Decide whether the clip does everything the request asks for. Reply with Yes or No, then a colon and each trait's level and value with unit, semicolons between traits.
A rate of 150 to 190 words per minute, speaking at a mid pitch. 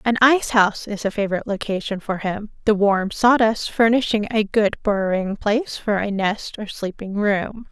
No: average, 180 wpm; high, 210 Hz